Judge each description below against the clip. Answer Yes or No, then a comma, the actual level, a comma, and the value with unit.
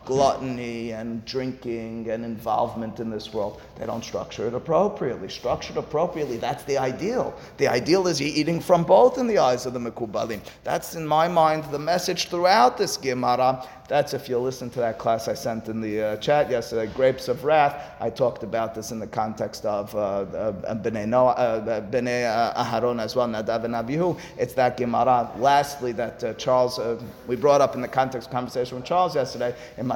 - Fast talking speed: No, average, 190 wpm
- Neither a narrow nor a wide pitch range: Yes, average, 3.6 semitones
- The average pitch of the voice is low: Yes, low, 125 Hz